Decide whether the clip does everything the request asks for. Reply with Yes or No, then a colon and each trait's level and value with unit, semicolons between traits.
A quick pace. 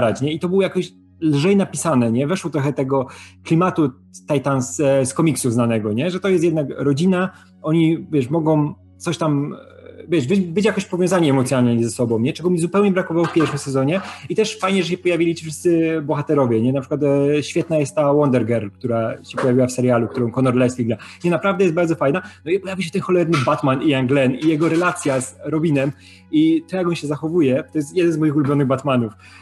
Yes: fast, 205 wpm